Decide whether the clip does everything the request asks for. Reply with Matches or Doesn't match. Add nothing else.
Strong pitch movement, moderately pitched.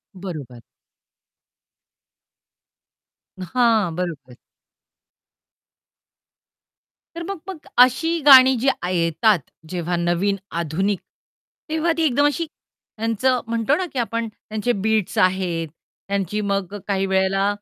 Doesn't match